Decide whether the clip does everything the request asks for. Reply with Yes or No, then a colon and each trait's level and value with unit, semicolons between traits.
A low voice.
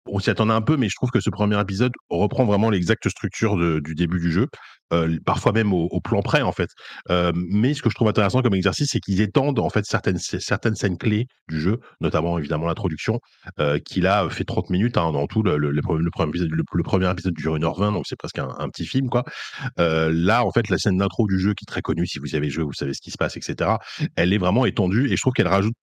Yes: low, 100 Hz